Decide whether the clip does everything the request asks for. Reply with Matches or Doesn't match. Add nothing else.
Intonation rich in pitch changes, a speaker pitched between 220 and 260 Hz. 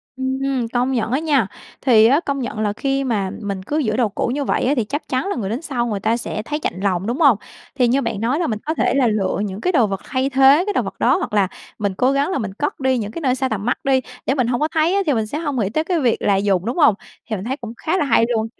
Doesn't match